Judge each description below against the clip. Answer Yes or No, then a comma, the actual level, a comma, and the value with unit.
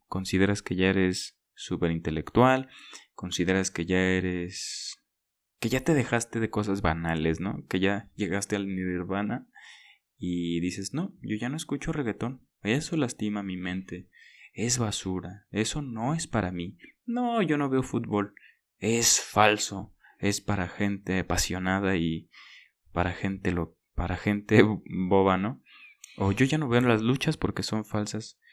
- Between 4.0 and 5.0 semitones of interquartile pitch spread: Yes, average, 4.3 semitones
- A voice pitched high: No, low, 100 Hz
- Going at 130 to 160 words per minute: Yes, average, 150 wpm